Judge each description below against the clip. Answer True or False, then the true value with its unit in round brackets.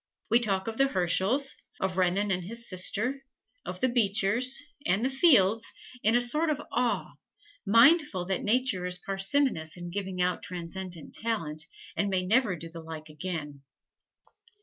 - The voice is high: True (195 Hz)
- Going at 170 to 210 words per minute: False (155 wpm)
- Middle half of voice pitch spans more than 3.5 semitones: True (5.1 semitones)